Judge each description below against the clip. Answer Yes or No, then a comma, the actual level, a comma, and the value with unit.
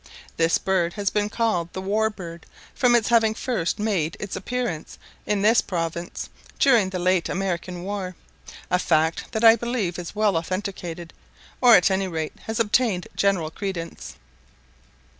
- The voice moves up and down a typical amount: Yes, average, 4.1 semitones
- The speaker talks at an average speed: Yes, average, 155 wpm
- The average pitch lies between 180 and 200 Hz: Yes, high, 190 Hz